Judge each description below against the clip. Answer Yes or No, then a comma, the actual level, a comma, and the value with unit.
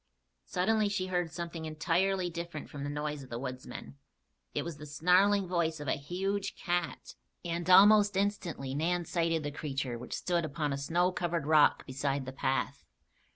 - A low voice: No, medium, 165 Hz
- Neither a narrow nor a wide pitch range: Yes, average, 3.8 semitones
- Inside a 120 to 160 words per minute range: No, average, 170 wpm